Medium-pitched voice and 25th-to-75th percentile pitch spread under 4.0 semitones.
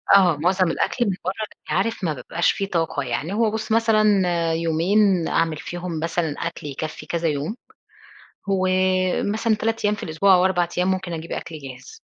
Yes: medium, 180 Hz; average, 3.5 semitones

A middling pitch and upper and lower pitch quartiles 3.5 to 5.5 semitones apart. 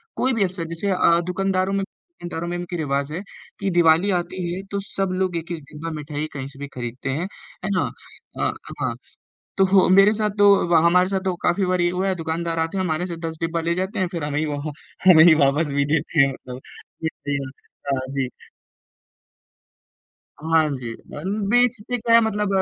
Yes: medium, 170 Hz; average, 3.8 semitones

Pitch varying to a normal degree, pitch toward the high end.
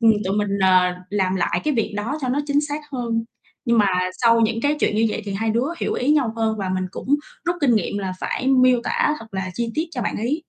Yes: average, 4.2 semitones; high, 230 Hz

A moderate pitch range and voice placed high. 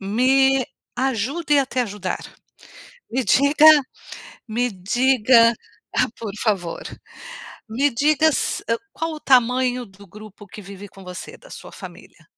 Yes: average, 4.6 semitones; high, 245 Hz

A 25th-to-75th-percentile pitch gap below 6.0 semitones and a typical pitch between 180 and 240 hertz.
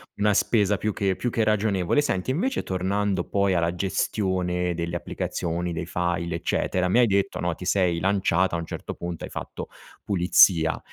No: average, 2.7 semitones; very low, 95 Hz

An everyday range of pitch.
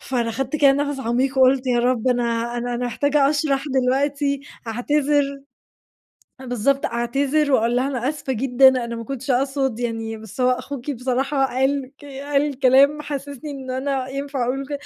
No: narrow, 2.3 semitones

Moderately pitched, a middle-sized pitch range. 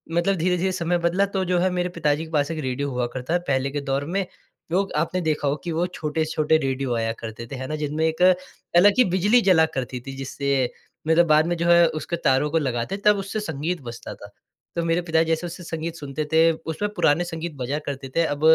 Yes: medium, 160 Hz; average, 3.8 semitones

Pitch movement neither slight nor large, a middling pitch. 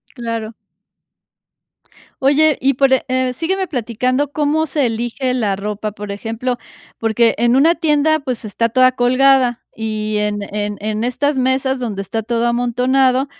No: average, 3.3 semitones; very high, 250 Hz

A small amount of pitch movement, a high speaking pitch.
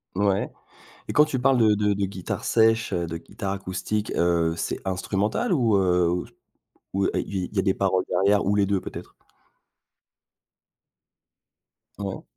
No: narrow, 2.3 semitones; low, 100 Hz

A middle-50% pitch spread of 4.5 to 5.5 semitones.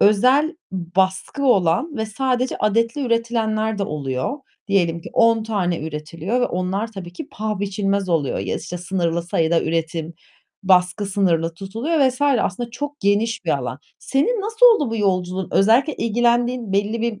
Yes: average, 5.1 semitones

